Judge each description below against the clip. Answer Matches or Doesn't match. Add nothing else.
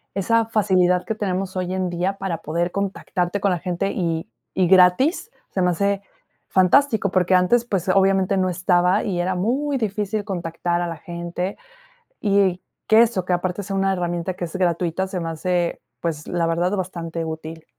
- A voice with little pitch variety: Matches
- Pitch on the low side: Doesn't match